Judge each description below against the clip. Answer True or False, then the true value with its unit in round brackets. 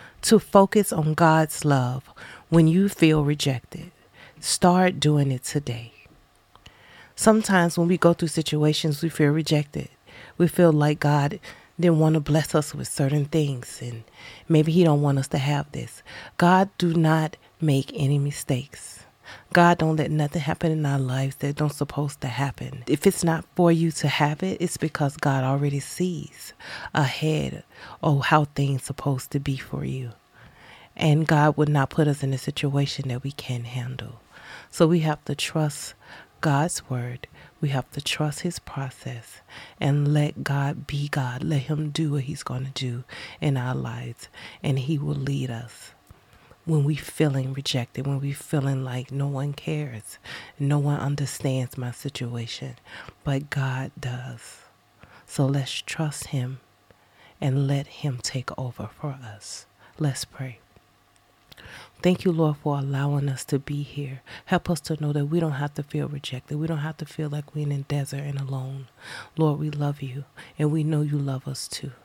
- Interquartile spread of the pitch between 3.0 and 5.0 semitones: False (2.6 semitones)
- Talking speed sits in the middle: True (170 wpm)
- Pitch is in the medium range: True (145 Hz)